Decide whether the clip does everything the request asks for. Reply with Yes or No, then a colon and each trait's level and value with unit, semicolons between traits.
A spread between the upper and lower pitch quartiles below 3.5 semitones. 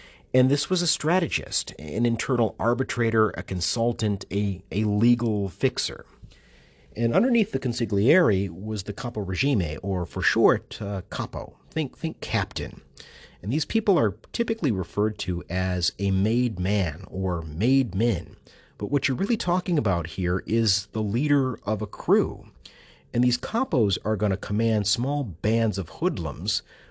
No: average, 4.8 semitones